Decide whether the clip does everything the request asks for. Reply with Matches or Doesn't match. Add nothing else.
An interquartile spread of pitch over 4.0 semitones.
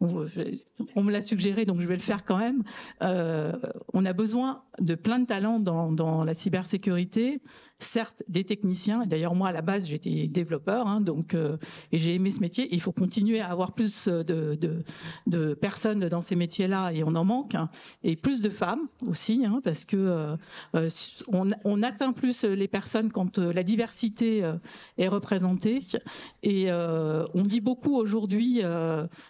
Matches